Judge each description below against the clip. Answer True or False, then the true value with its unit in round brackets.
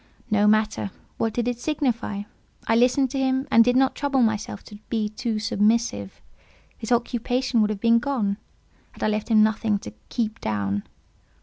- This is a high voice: True (225 Hz)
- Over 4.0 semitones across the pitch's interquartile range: False (2.8 semitones)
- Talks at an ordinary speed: True (175 wpm)